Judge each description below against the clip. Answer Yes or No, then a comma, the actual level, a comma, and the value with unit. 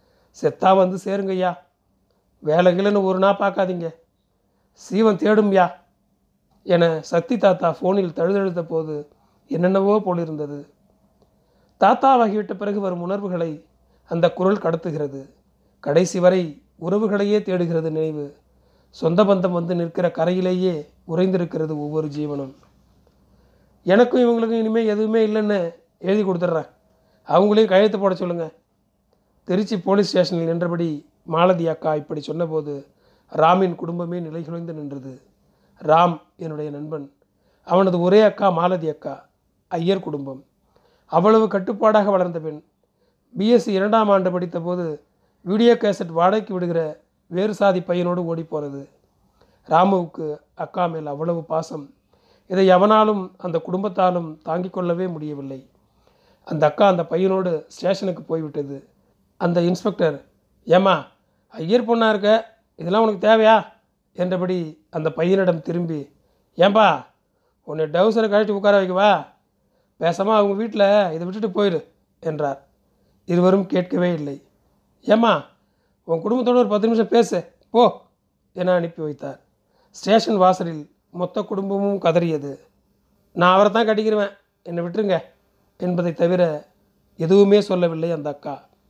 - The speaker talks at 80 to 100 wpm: No, average, 110 wpm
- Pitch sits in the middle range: Yes, medium, 180 Hz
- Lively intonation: No, average, 3.8 semitones